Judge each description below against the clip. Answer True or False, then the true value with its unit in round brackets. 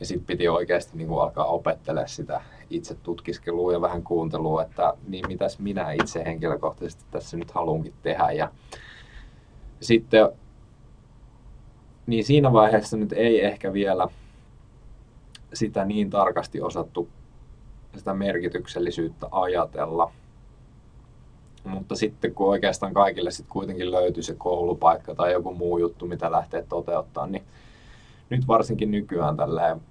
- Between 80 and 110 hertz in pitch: True (100 Hz)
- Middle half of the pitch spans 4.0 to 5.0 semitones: True (4.3 semitones)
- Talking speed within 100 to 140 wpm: True (120 wpm)